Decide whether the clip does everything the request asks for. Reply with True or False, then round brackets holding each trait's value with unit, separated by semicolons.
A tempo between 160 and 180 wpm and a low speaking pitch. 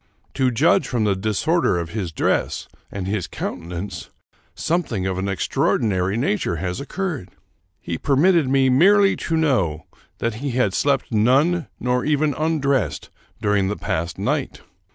False (145 wpm; 120 Hz)